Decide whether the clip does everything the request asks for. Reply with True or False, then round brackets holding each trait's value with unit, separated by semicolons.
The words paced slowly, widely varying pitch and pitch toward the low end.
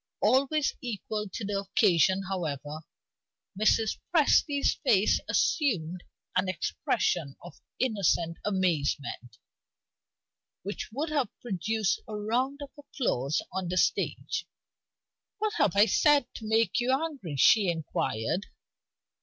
False (110 wpm; 6.5 semitones; 205 Hz)